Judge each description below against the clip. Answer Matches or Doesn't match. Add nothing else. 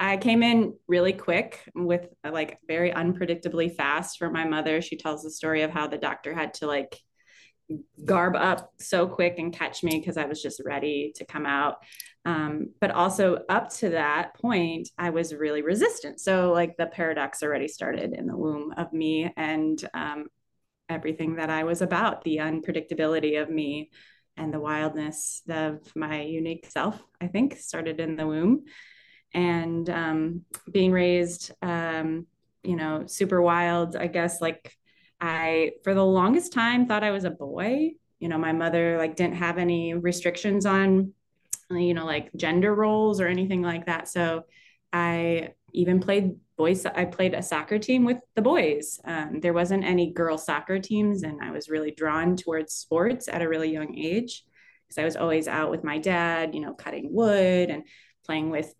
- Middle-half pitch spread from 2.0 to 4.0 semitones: Matches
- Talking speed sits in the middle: Matches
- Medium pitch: Matches